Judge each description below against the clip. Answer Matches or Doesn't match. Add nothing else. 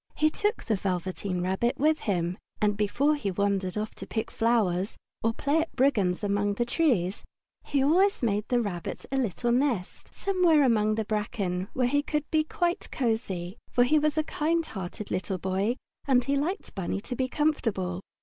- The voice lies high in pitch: Matches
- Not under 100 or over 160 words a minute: Doesn't match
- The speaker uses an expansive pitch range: Matches